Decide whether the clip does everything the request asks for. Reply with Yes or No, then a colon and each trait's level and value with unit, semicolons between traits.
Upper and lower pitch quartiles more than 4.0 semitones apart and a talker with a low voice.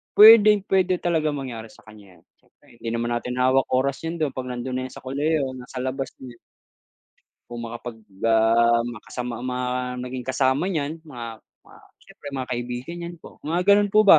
Yes: average, 4.7 semitones; low, 130 Hz